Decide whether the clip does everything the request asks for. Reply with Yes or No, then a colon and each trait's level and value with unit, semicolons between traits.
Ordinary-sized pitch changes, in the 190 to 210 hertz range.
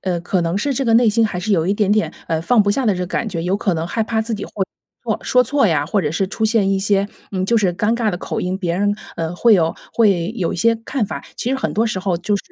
Yes: average, 3.9 semitones; high, 200 Hz